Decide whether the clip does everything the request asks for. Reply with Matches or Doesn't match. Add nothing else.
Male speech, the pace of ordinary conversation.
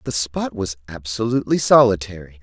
Doesn't match